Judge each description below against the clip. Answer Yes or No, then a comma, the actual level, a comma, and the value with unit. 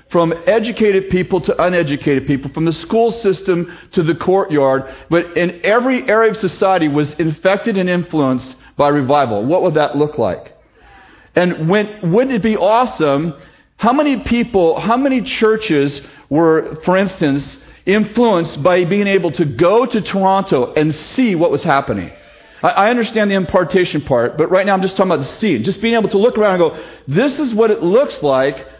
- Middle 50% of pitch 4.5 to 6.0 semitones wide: Yes, wide, 5.5 semitones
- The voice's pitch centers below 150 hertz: No, medium, 180 Hz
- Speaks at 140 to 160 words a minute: No, average, 180 wpm